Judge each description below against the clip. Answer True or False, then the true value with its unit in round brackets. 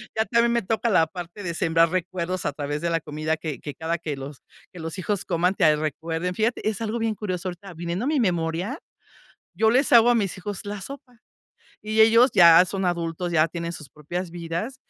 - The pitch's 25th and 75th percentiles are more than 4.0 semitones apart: True (4.8 semitones)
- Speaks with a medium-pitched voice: True (180 Hz)